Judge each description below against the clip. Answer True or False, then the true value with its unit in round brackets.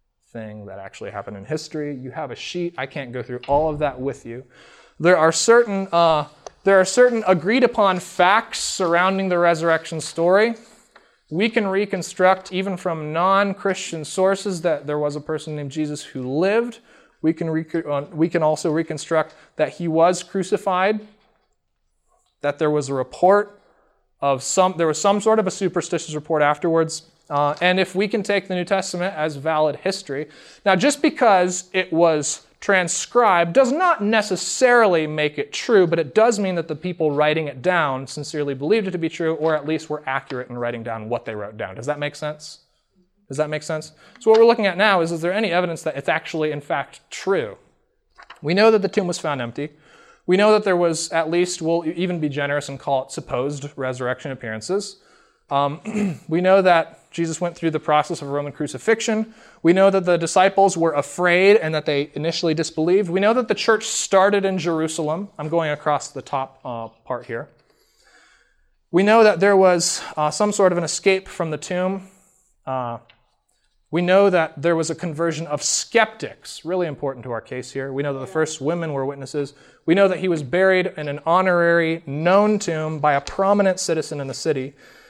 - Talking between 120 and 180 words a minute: False (190 wpm)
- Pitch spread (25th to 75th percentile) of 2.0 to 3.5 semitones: False (4.3 semitones)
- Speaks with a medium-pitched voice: True (165 Hz)